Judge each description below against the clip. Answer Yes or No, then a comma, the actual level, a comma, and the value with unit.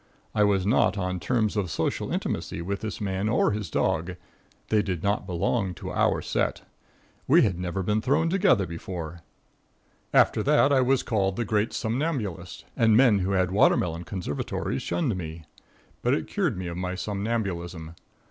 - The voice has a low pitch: Yes, low, 100 Hz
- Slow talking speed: No, average, 165 wpm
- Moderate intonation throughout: Yes, average, 3.9 semitones